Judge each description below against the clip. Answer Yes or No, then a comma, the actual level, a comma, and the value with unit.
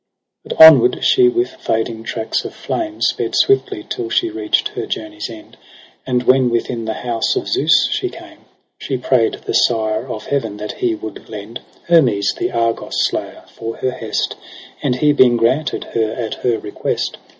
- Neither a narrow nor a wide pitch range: No, wide, 6.0 semitones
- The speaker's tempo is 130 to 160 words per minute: No, average, 180 wpm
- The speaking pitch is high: No, low, 125 Hz